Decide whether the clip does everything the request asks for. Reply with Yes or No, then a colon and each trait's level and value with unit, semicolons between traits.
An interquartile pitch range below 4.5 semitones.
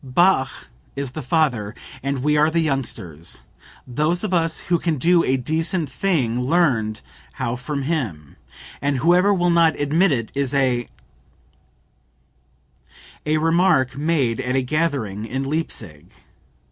No: average, 4.9 semitones